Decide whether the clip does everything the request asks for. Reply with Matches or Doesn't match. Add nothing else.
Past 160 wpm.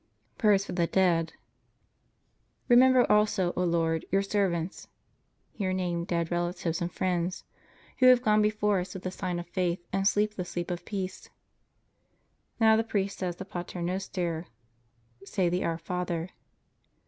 Doesn't match